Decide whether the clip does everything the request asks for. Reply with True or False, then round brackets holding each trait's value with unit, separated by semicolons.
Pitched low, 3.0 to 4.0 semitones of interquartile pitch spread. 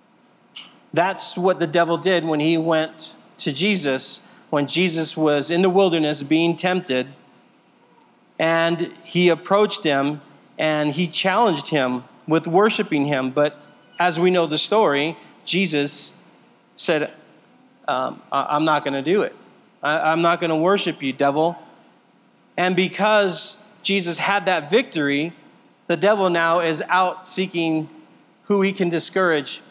False (170 Hz; 3.3 semitones)